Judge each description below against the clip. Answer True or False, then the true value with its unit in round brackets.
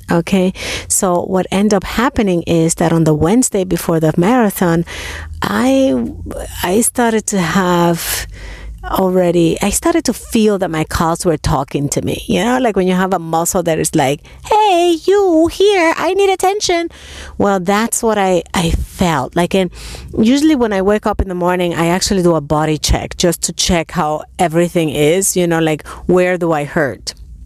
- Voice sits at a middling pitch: True (180 Hz)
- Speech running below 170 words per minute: False (180 wpm)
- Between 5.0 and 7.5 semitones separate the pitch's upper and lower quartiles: True (5.3 semitones)